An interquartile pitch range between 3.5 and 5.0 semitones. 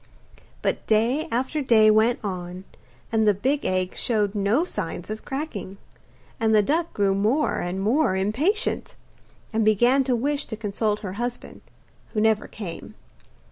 Yes: average, 4.2 semitones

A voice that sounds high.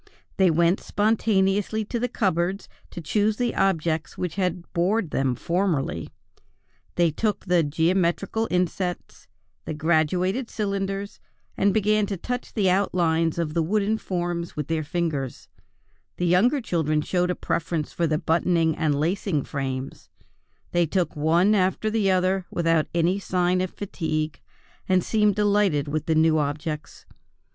No: medium, 175 Hz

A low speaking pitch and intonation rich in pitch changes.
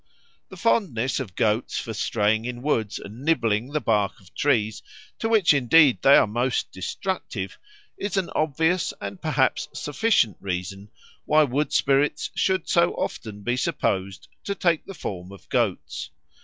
Yes: low, 125 Hz; wide, 7.2 semitones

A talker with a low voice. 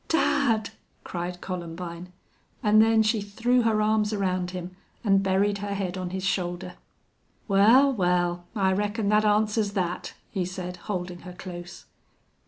No: high, 195 Hz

